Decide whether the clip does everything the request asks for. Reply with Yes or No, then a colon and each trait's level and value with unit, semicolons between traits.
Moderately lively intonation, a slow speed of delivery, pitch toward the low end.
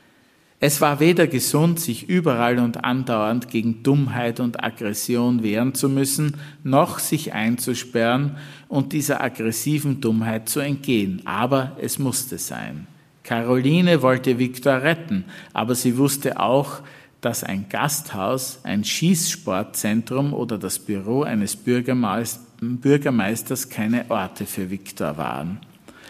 Yes: average, 3.9 semitones; slow, 120 wpm; low, 130 Hz